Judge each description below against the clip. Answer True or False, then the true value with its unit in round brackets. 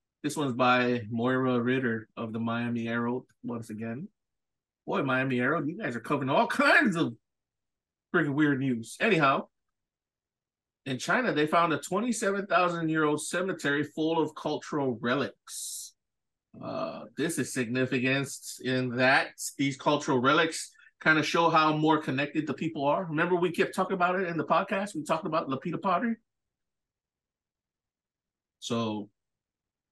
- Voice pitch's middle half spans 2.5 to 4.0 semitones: False (4.8 semitones)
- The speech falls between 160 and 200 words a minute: False (140 wpm)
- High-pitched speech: False (140 Hz)